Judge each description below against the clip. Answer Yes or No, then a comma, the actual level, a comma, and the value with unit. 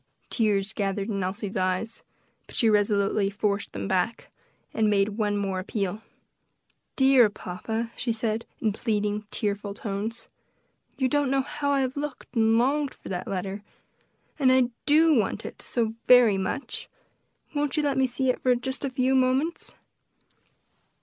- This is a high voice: Yes, high, 220 Hz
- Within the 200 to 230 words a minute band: No, average, 155 wpm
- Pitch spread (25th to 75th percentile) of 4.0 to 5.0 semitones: Yes, average, 4.4 semitones